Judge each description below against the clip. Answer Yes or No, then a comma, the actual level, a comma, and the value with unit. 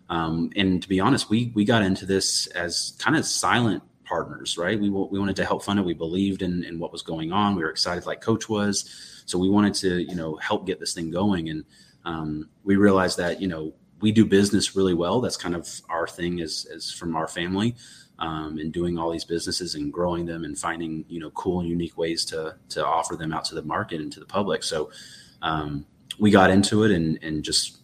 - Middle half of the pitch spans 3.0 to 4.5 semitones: Yes, average, 3.3 semitones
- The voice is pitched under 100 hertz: Yes, very low, 90 Hz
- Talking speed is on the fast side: Yes, fast, 235 wpm